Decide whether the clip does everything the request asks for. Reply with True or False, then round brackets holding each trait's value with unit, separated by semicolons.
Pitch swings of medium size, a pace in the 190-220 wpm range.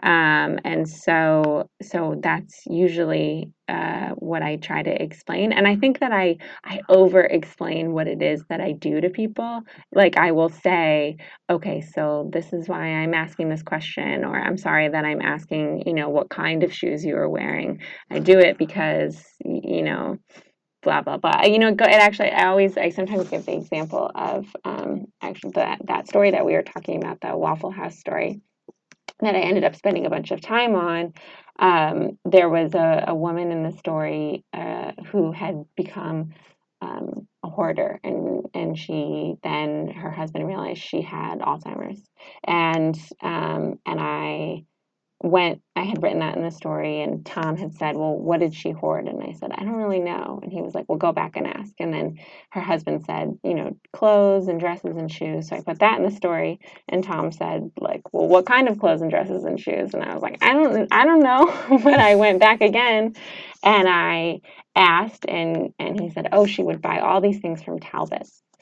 True (4.3 semitones; 200 wpm)